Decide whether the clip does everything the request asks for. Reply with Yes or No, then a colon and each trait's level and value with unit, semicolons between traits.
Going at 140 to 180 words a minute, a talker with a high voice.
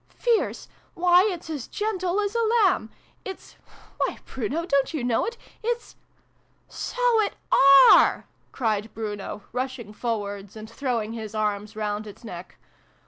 Yes: average, 150 wpm; very high, 250 Hz